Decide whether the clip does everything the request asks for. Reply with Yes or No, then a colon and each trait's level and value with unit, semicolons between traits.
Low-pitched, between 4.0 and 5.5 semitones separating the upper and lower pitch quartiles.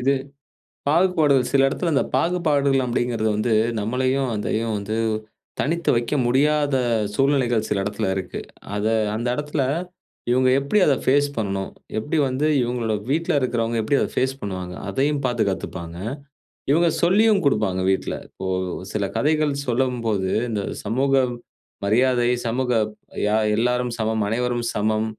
Yes: low, 125 Hz; average, 4.4 semitones